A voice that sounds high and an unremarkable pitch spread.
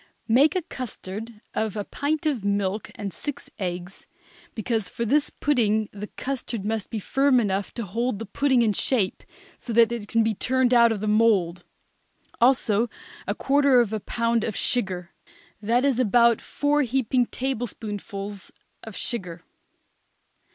Yes: high, 225 Hz; average, 3.7 semitones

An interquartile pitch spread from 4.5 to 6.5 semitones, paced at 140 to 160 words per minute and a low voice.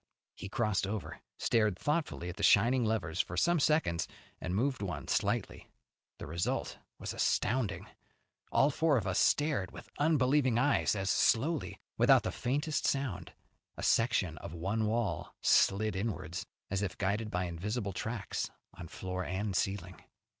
Yes: wide, 5.6 semitones; average, 150 wpm; low, 105 Hz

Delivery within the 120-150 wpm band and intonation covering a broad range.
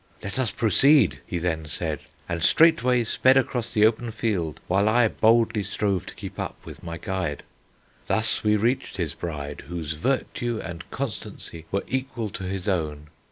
No: average, 165 wpm; wide, 5.8 semitones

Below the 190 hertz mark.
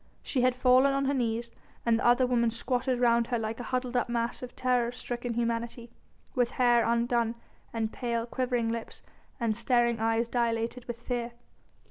No: high, 240 Hz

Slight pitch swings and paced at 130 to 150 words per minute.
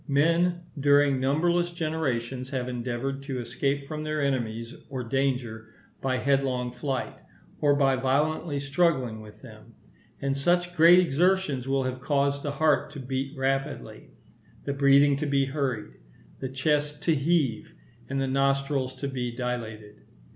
Yes: narrow, 2.3 semitones; average, 145 wpm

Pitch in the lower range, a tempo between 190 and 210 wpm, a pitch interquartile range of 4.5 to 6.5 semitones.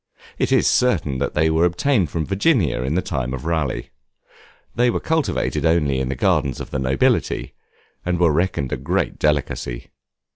No: very low, 80 Hz; average, 170 wpm; average, 4.8 semitones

